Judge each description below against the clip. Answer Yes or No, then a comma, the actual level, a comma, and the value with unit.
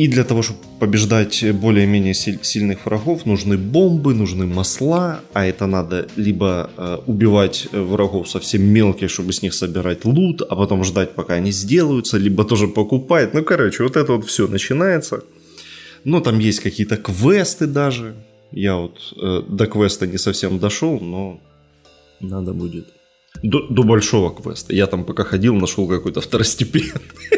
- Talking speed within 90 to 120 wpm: No, average, 150 wpm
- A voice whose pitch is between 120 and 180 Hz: No, low, 105 Hz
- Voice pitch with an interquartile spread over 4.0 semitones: Yes, average, 4.6 semitones